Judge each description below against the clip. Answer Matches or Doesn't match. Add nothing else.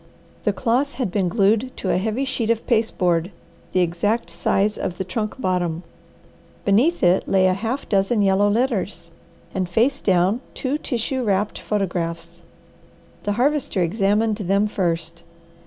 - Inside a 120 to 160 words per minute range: Matches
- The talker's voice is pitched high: Matches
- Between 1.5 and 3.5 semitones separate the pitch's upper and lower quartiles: Doesn't match